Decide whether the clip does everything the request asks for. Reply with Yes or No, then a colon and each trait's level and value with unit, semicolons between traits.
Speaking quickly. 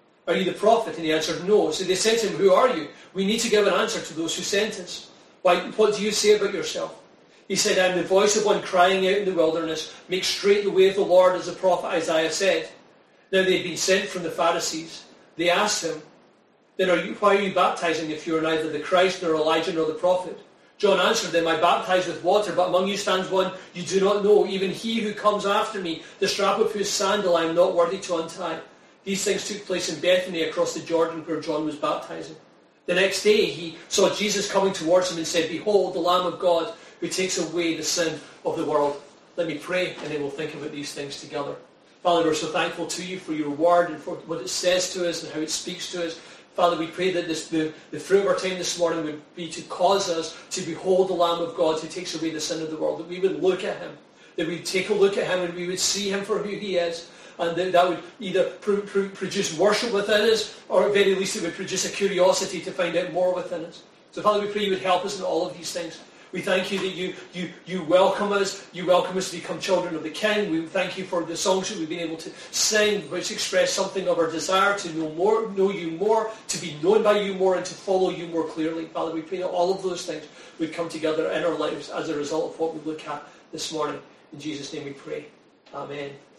Yes: fast, 255 wpm